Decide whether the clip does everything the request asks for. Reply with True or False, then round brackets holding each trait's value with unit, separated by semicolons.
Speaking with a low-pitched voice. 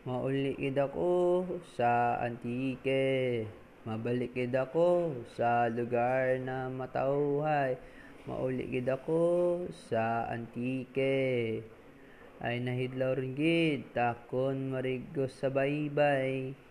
True (130 Hz)